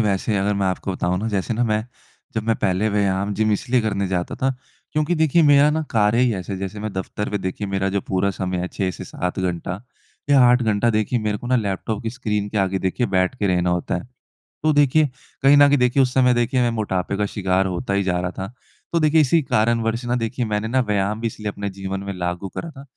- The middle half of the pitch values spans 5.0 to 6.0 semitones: No, average, 4.2 semitones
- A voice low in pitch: Yes, low, 105 Hz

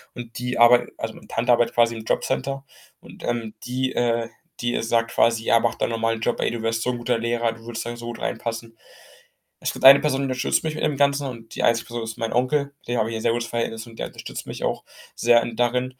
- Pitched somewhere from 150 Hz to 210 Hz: No, low, 120 Hz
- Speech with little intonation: Yes, narrow, 1.4 semitones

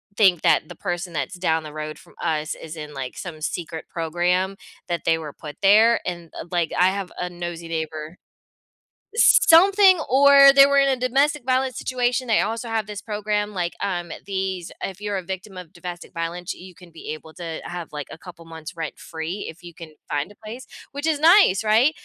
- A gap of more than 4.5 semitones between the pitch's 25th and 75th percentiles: Yes, average, 5.2 semitones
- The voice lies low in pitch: No, medium, 180 Hz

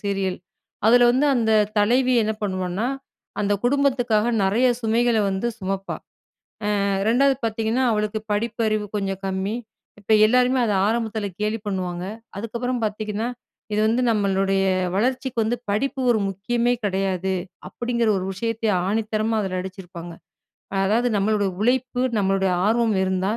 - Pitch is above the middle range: Yes, high, 215 Hz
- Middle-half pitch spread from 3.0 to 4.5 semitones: Yes, average, 3.4 semitones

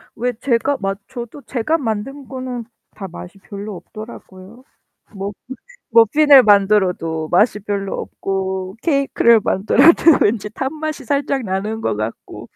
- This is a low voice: No, high, 220 Hz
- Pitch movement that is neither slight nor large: Yes, average, 5.0 semitones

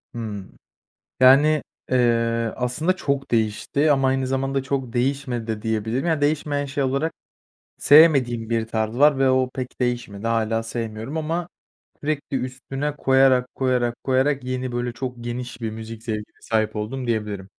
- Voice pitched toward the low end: Yes, low, 125 Hz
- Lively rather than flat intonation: No, average, 3.2 semitones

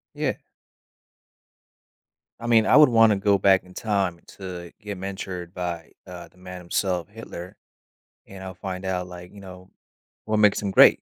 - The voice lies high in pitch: No, very low, 95 Hz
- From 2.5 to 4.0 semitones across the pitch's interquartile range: No, narrow, 2.1 semitones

